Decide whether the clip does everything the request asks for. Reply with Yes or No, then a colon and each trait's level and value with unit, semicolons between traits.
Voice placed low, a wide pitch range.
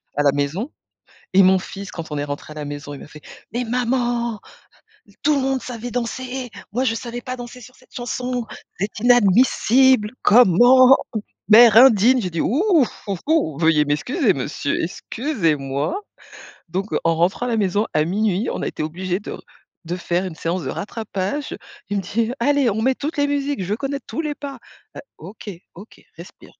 No: high, 225 Hz; wide, 6.2 semitones